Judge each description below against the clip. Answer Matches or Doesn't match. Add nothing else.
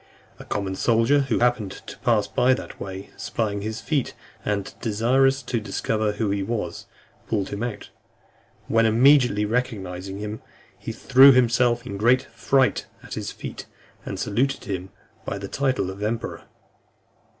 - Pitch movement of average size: Matches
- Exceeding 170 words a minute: Doesn't match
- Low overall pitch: Matches